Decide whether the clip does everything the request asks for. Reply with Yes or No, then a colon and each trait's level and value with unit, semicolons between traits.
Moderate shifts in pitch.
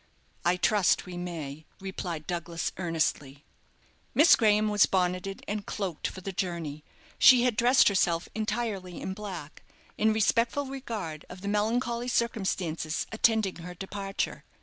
Yes: average, 4.0 semitones